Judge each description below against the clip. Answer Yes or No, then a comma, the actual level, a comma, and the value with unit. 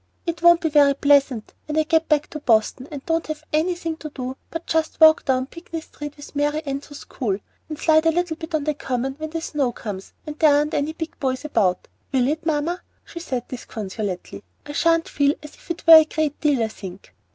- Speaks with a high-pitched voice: Yes, very high, 300 Hz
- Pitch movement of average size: Yes, average, 3.3 semitones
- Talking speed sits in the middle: No, fast, 225 wpm